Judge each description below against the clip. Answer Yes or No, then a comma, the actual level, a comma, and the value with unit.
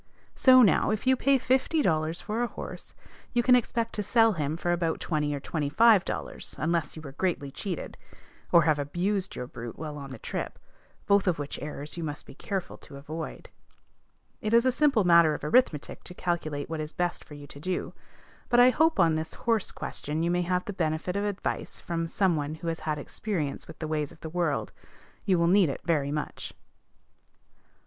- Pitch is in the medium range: Yes, medium, 170 Hz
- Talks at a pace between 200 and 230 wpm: Yes, fast, 205 wpm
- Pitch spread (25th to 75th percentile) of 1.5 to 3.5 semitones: No, average, 5.1 semitones